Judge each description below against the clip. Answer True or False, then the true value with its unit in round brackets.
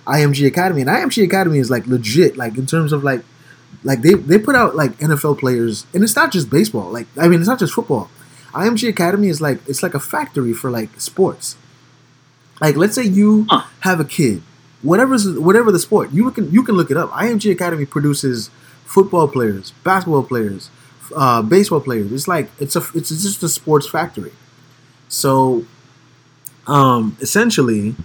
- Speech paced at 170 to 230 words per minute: True (180 wpm)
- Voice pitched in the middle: True (150 Hz)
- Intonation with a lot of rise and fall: True (6.0 semitones)